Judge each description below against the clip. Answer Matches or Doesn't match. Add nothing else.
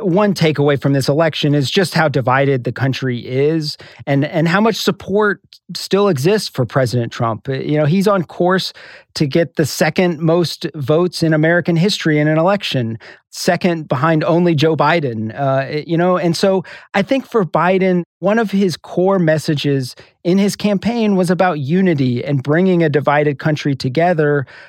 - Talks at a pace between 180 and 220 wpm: Doesn't match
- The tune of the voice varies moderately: Matches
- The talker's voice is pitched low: Doesn't match